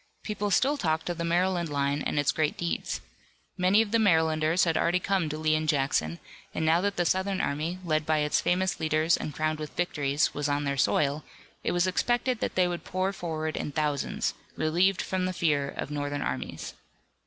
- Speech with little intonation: No, average, 3.4 semitones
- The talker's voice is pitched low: No, medium, 160 Hz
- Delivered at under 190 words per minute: No, average, 200 wpm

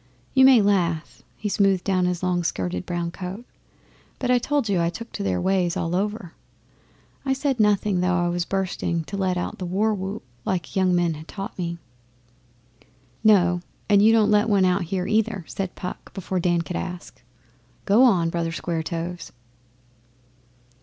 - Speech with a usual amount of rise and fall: Yes, average, 3.0 semitones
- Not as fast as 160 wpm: No, average, 180 wpm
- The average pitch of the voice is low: No, medium, 185 Hz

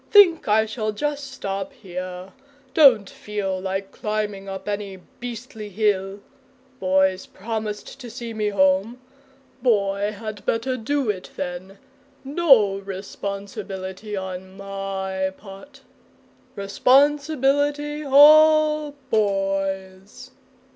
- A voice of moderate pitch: No, high, 210 Hz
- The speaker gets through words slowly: Yes, slow, 100 wpm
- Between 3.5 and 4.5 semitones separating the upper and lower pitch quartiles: No, average, 5.0 semitones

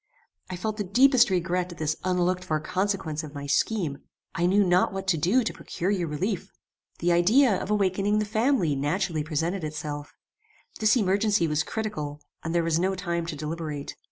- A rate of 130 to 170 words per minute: No, average, 185 wpm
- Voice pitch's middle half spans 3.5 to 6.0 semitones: Yes, average, 4.5 semitones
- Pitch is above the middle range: No, medium, 180 Hz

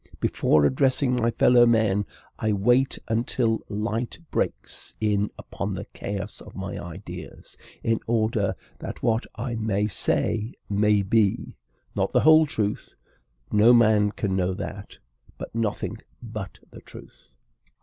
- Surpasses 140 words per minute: No, slow, 135 wpm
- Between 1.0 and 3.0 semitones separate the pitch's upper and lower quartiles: Yes, narrow, 2.4 semitones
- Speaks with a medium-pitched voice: No, low, 110 Hz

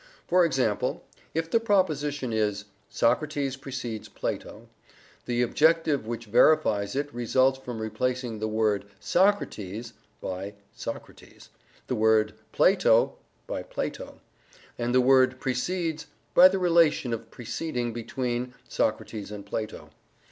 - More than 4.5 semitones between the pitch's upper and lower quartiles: Yes, average, 5.1 semitones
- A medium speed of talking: No, slow, 120 wpm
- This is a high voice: No, low, 125 Hz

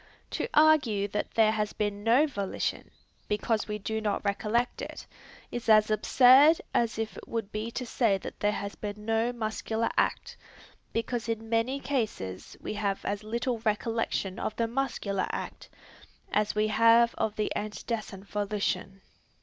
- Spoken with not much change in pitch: Yes, narrow, 2.0 semitones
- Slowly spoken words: No, average, 155 wpm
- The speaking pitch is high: Yes, high, 220 Hz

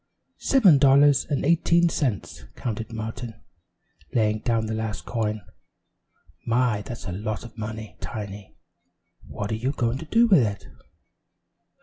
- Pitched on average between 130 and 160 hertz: No, low, 115 Hz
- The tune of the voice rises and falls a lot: No, average, 4.1 semitones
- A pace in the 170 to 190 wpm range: No, slow, 135 wpm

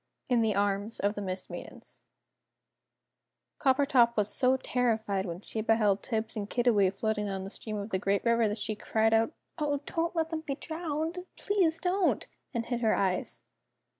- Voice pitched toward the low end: No, high, 225 Hz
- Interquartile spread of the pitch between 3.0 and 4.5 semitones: No, average, 5.1 semitones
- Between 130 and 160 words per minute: No, average, 175 wpm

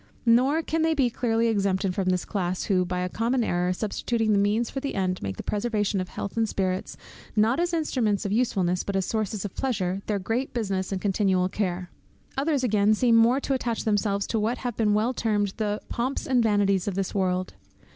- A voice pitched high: Yes, high, 210 Hz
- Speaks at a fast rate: Yes, fast, 210 wpm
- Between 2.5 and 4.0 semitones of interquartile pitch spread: Yes, average, 3.7 semitones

